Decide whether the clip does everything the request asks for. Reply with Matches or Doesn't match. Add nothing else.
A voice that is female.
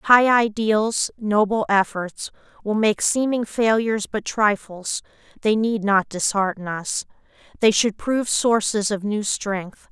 Matches